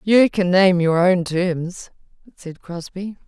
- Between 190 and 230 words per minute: No, average, 145 wpm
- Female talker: Yes, female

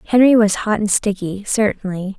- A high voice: Yes, high, 205 Hz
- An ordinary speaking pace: Yes, average, 165 wpm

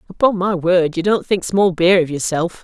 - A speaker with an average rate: No, fast, 230 wpm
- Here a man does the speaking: No, female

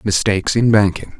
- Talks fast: No, average, 150 wpm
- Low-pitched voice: Yes, low, 100 Hz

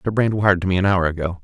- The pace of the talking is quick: Yes, fast, 335 wpm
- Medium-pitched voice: No, very low, 95 Hz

